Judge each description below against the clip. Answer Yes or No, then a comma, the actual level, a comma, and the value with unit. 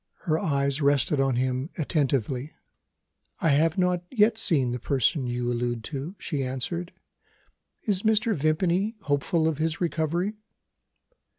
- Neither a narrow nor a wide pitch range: Yes, average, 4.8 semitones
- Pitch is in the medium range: Yes, medium, 155 Hz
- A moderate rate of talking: No, slow, 130 wpm